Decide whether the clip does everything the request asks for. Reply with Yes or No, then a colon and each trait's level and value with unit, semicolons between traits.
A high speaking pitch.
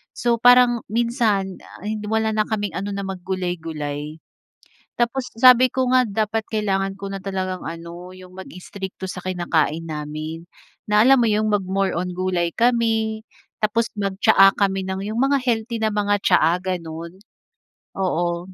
Yes: high, 195 Hz